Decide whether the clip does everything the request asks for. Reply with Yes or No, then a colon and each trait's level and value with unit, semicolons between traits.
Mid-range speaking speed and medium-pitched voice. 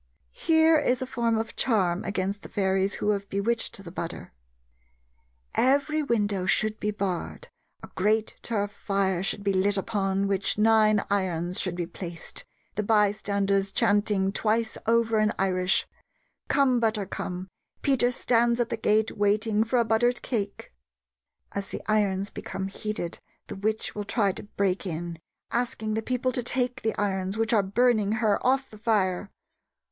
No: average, 160 wpm; high, 210 Hz